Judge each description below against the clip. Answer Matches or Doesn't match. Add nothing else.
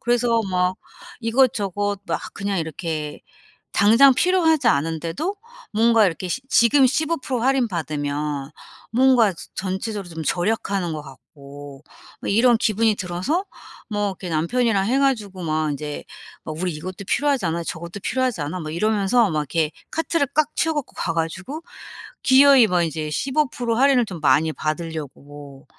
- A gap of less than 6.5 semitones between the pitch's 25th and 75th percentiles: Doesn't match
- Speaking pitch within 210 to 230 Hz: Doesn't match